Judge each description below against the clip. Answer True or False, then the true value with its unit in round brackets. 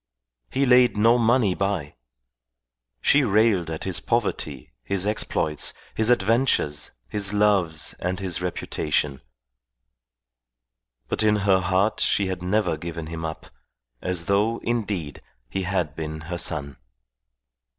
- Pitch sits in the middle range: False (95 Hz)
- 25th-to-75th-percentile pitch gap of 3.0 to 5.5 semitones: True (4.7 semitones)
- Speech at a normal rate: False (125 wpm)